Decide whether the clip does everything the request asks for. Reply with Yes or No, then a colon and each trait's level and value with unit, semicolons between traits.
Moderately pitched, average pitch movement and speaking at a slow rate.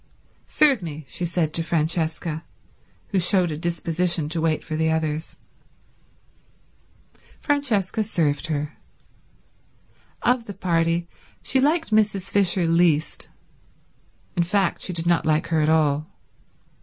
Yes: medium, 170 Hz; average, 3.2 semitones; slow, 125 wpm